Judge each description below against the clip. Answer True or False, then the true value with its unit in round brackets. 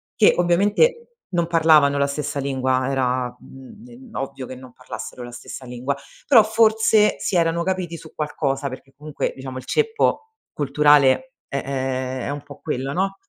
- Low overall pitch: False (145 Hz)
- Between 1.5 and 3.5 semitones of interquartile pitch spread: False (5.7 semitones)